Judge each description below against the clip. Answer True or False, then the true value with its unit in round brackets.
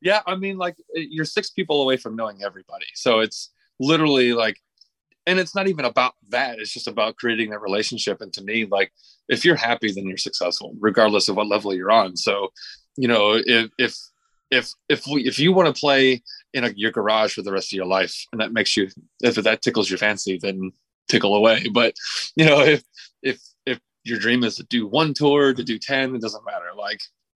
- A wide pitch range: True (5.7 semitones)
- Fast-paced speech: True (215 wpm)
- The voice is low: True (120 Hz)